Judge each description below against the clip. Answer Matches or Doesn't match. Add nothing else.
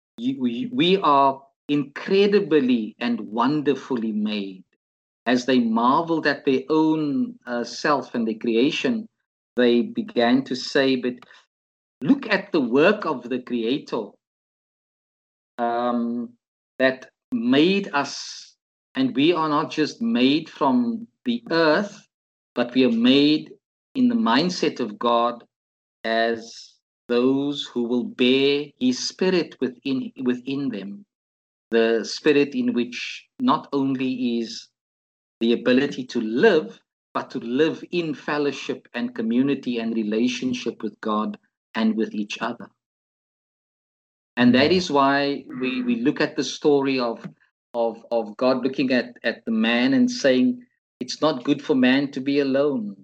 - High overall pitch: Doesn't match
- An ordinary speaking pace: Doesn't match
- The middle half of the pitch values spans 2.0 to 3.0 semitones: Doesn't match